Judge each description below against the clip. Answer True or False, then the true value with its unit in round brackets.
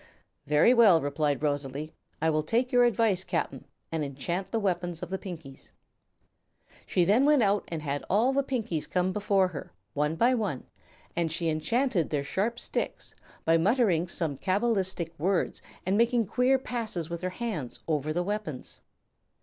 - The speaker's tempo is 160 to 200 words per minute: True (165 wpm)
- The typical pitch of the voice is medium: True (180 Hz)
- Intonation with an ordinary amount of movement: False (6.2 semitones)